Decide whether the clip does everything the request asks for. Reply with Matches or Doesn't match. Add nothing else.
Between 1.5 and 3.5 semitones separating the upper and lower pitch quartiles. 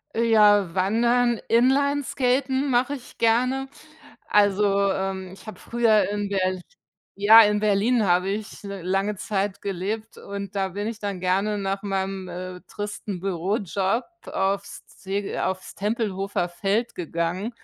Matches